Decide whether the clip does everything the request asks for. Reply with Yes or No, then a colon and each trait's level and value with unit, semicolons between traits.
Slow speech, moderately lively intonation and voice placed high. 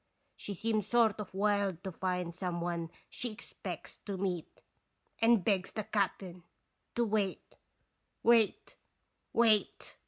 Yes: slow, 125 wpm; average, 3.1 semitones; high, 200 Hz